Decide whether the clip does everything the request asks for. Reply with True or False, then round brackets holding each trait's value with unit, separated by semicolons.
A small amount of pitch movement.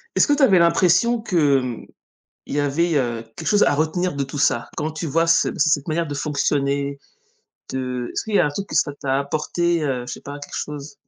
False (3.4 semitones)